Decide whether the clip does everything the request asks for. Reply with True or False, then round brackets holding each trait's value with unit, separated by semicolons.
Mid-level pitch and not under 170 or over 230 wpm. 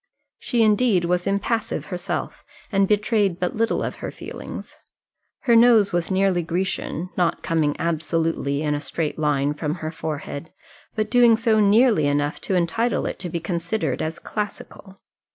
False (180 Hz; 155 wpm)